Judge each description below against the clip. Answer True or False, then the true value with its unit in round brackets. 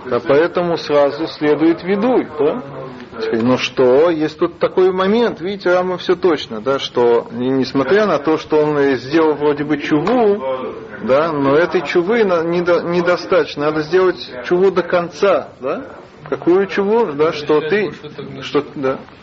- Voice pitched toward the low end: False (160 Hz)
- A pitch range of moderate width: True (4.9 semitones)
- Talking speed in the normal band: True (145 wpm)